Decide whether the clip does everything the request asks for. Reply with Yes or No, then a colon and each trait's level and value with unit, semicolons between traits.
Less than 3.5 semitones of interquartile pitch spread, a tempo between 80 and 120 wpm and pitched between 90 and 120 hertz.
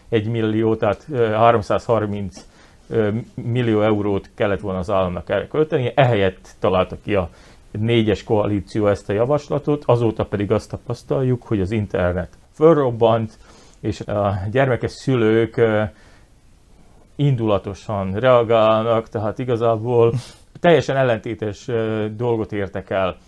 Yes: average, 2.8 semitones; average, 110 wpm; low, 110 Hz